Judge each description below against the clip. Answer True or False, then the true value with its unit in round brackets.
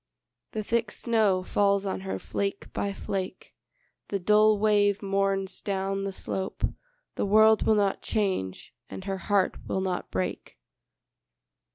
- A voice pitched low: False (200 Hz)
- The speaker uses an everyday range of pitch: False (1.6 semitones)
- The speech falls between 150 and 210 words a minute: False (140 wpm)